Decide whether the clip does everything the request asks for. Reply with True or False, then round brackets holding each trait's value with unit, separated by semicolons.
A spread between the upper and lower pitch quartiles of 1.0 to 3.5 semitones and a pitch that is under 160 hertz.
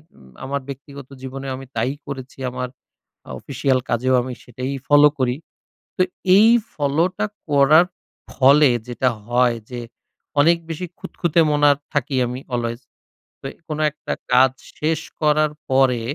True (2.9 semitones; 135 Hz)